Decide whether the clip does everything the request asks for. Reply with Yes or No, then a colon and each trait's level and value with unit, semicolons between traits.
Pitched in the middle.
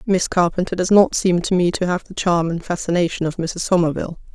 Yes: medium, 175 Hz